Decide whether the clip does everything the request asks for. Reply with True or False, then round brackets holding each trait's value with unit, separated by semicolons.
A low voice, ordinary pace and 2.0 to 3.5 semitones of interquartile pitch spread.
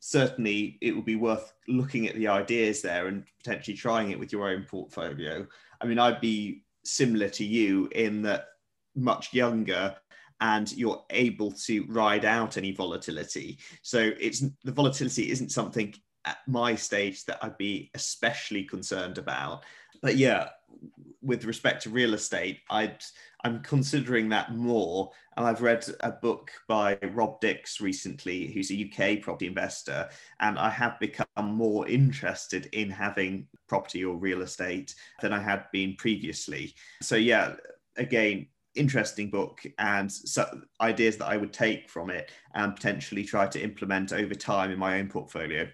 True (110 Hz; 155 wpm; 2.8 semitones)